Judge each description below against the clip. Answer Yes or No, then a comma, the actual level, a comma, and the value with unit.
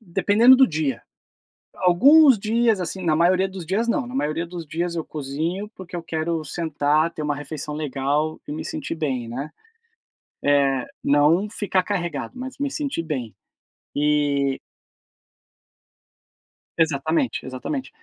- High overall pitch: No, medium, 165 Hz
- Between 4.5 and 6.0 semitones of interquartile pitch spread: Yes, average, 4.9 semitones